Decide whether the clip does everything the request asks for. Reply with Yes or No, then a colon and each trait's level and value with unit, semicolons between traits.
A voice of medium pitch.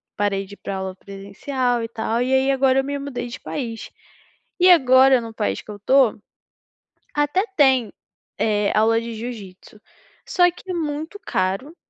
No: high, 245 Hz